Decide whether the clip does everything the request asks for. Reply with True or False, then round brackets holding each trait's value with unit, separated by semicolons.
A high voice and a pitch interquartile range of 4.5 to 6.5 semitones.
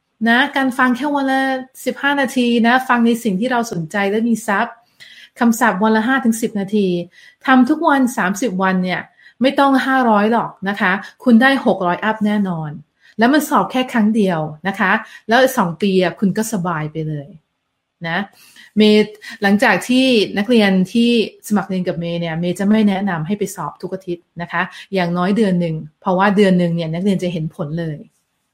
True (205 Hz; 4.8 semitones)